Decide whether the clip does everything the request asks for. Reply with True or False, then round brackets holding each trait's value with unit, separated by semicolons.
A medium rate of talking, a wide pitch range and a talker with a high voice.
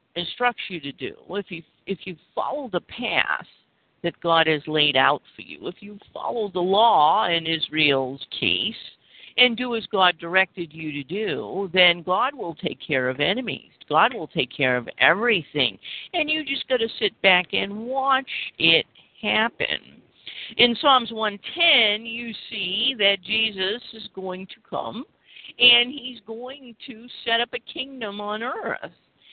True (160 wpm; 5.7 semitones; 205 Hz)